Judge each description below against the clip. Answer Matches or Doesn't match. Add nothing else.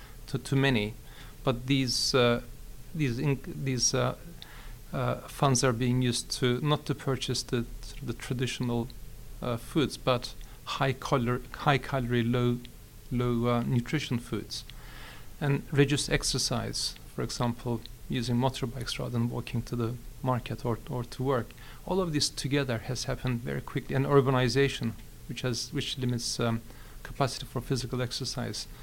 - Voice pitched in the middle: Doesn't match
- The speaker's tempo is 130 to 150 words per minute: Matches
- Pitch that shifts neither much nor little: Doesn't match